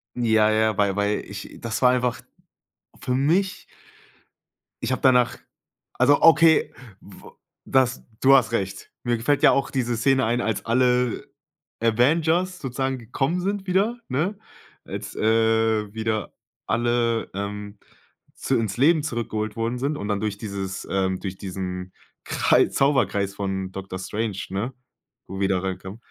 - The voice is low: Yes, low, 115 Hz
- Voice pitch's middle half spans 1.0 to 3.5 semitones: No, average, 4.6 semitones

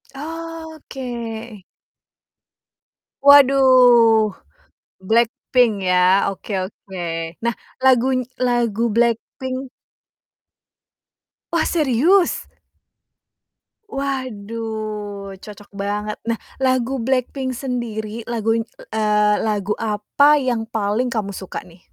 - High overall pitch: Yes, high, 235 Hz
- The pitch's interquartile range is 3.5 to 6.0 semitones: Yes, average, 3.8 semitones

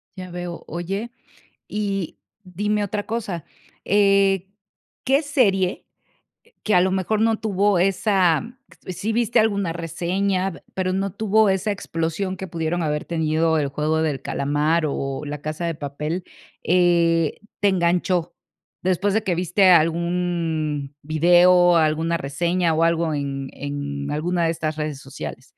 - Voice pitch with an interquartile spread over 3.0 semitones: Yes, average, 3.5 semitones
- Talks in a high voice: No, medium, 175 Hz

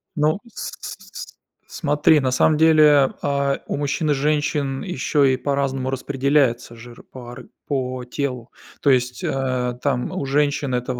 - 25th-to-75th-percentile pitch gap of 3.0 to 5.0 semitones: No, narrow, 2.4 semitones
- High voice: No, low, 135 Hz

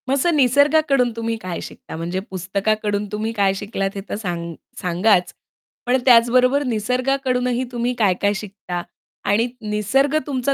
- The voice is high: Yes, high, 225 Hz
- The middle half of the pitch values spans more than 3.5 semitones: Yes, average, 4.2 semitones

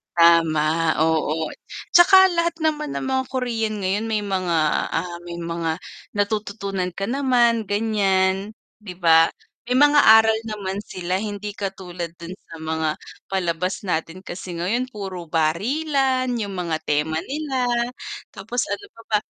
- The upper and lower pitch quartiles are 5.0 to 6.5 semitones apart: Yes, average, 5.3 semitones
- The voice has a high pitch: Yes, high, 195 Hz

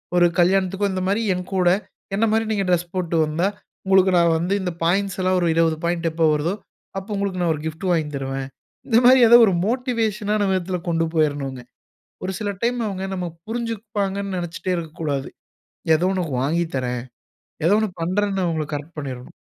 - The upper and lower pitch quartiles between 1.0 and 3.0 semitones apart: No, average, 3.5 semitones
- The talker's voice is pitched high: No, medium, 180 Hz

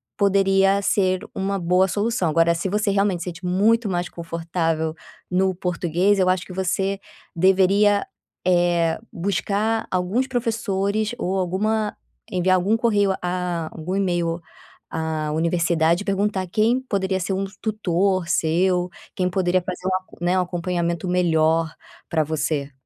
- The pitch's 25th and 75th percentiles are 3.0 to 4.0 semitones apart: No, narrow, 2.5 semitones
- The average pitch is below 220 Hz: Yes, medium, 185 Hz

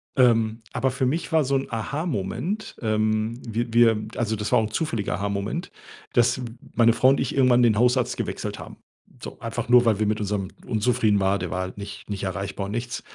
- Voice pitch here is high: No, low, 115 Hz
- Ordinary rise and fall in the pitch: Yes, average, 3.2 semitones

